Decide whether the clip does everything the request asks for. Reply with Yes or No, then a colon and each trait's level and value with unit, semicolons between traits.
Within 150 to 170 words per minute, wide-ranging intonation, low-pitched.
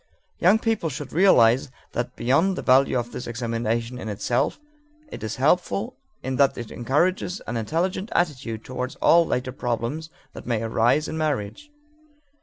Yes: average, 160 wpm; wide, 5.9 semitones; low, 130 Hz